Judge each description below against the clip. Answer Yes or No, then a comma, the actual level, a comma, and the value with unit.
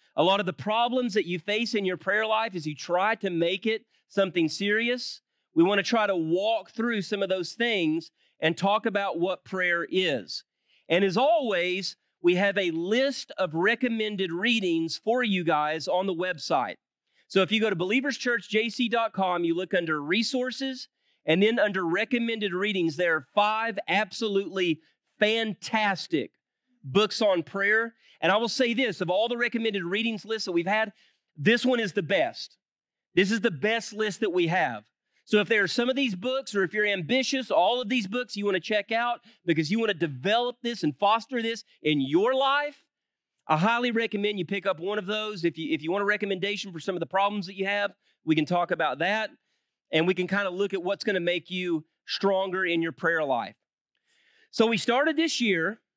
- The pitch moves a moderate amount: Yes, average, 4.2 semitones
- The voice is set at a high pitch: Yes, high, 210 Hz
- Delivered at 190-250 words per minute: Yes, average, 200 wpm